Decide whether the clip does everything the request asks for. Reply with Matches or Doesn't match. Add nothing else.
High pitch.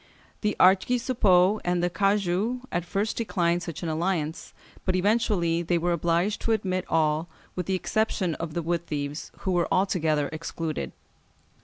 Doesn't match